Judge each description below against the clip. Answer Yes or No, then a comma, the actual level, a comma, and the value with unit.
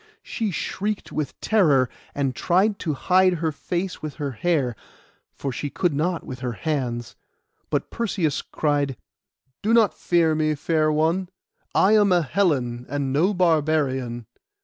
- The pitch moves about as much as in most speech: Yes, average, 4.7 semitones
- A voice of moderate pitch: Yes, medium, 155 Hz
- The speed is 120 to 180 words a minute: Yes, average, 150 wpm